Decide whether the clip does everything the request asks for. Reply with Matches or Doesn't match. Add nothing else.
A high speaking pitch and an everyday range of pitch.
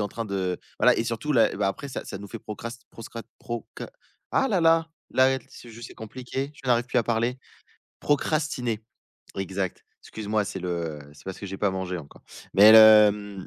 Doesn't match